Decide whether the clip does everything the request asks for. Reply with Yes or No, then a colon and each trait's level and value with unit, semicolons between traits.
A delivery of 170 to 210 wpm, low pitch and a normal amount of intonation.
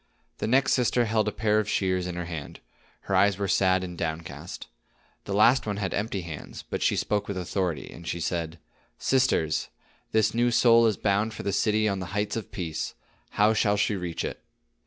Yes: average, 200 wpm; low, 100 Hz; average, 3.5 semitones